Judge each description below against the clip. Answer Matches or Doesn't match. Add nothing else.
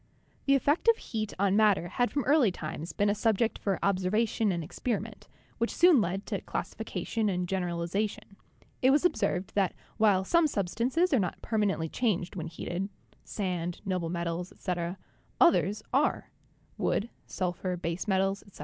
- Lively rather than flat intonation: Doesn't match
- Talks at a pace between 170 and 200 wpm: Doesn't match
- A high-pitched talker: Matches